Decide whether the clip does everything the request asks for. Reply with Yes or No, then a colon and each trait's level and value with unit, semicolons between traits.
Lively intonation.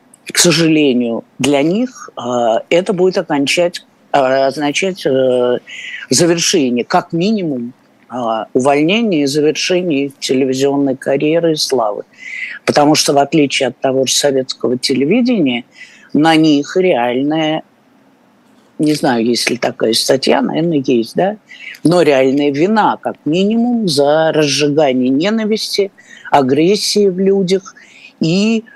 Yes: wide, 6.0 semitones